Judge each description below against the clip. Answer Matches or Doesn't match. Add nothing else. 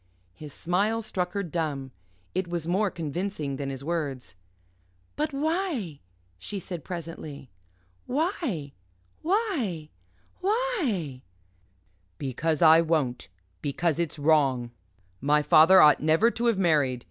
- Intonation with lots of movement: Matches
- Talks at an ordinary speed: Doesn't match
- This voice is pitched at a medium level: Matches